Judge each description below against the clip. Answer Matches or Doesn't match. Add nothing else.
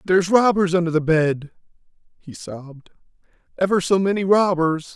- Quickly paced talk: Doesn't match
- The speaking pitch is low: Doesn't match